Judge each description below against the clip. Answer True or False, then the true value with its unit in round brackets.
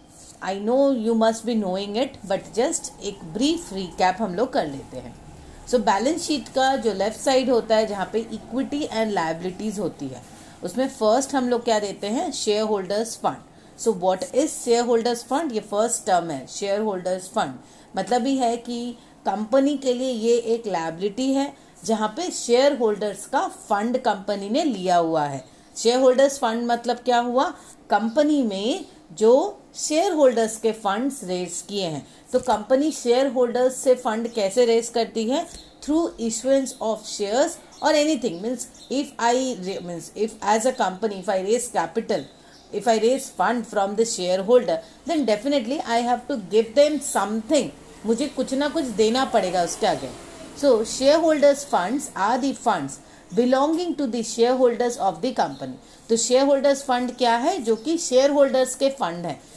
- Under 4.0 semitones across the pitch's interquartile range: False (4.4 semitones)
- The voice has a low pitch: False (235 Hz)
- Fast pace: False (175 wpm)